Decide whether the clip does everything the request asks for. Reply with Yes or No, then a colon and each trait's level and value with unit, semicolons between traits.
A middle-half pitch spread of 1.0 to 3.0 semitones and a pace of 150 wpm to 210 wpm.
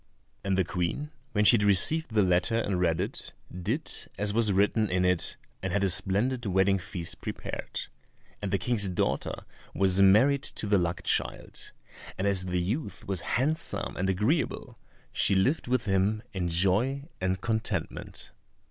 No: average, 3.5 semitones; average, 165 wpm